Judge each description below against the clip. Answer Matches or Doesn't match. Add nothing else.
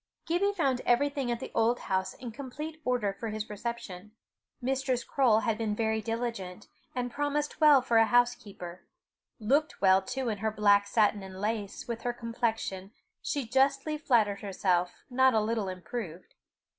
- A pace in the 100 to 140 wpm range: Doesn't match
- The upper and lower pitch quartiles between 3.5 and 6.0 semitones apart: Matches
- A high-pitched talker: Matches